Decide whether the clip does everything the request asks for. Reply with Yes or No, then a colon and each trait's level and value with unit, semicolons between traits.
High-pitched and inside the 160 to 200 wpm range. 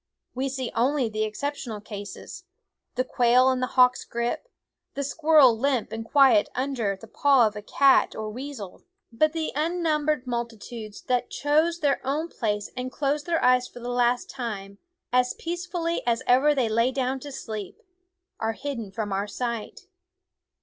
Yes: very high, 250 Hz; average, 165 wpm